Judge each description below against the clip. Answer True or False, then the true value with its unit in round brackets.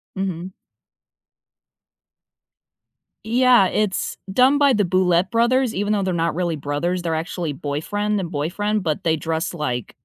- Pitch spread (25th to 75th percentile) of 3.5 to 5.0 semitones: True (4.5 semitones)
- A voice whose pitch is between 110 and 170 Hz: False (185 Hz)